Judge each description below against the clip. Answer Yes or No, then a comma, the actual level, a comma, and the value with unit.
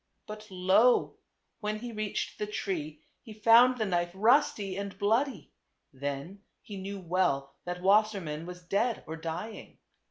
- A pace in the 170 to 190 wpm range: No, average, 140 wpm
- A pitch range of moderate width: Yes, average, 3.4 semitones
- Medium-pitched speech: No, high, 195 Hz